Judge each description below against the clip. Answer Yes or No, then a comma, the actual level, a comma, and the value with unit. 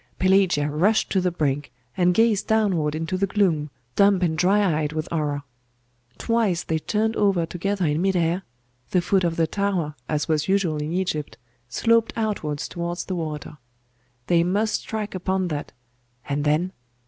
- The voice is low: No, medium, 175 Hz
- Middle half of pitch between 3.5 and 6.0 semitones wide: Yes, average, 4.3 semitones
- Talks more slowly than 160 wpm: No, average, 165 wpm